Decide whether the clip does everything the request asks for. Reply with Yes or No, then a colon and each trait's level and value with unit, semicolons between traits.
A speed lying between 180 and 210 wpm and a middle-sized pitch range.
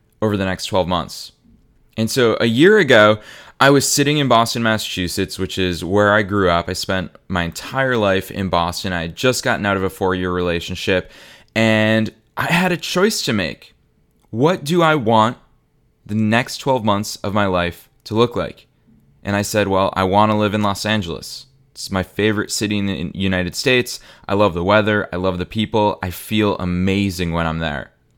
Yes: average, 200 wpm; average, 3.4 semitones